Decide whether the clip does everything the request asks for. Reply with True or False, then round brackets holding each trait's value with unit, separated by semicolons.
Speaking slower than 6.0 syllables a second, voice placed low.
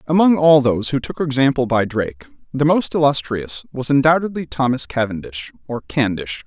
True (5.3 syllables/s; 130 Hz)